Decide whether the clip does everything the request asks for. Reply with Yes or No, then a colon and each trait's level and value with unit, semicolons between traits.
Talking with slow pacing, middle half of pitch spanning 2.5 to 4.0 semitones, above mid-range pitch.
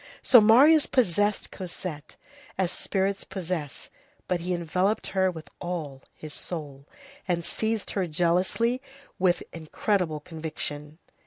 No: slow, 115 wpm; average, 3.7 semitones; medium, 180 Hz